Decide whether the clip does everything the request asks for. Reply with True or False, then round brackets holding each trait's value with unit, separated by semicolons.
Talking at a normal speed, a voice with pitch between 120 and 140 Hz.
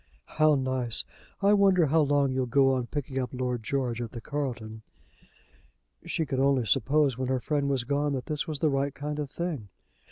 True (195 wpm; 135 Hz)